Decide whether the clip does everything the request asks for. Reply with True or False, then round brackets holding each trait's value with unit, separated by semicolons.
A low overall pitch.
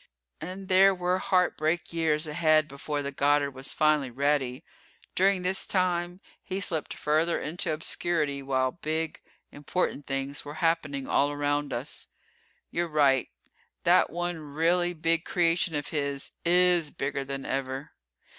False (155 Hz)